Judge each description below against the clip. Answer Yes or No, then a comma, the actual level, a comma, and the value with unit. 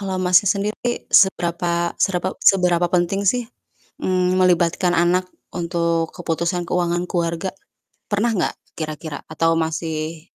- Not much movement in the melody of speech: Yes, narrow, 1.8 semitones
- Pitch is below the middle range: No, medium, 175 Hz